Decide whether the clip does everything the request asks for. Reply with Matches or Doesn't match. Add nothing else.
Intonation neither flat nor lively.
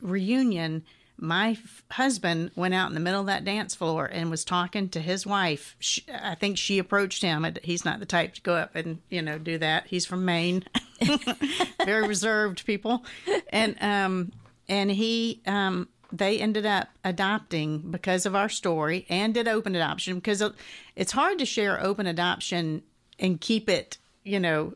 Matches